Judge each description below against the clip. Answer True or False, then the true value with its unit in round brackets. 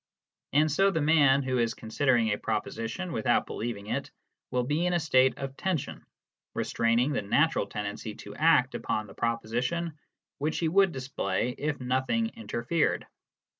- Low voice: True (130 Hz)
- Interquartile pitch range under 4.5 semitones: False (5.5 semitones)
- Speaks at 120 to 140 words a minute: False (155 wpm)